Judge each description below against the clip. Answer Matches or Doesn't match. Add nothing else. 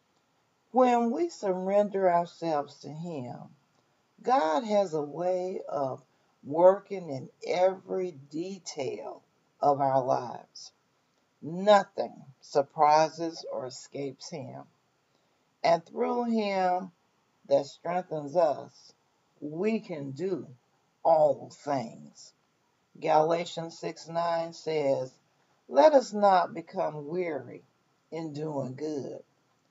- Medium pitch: Matches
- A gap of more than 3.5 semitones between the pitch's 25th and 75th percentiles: Matches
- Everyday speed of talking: Doesn't match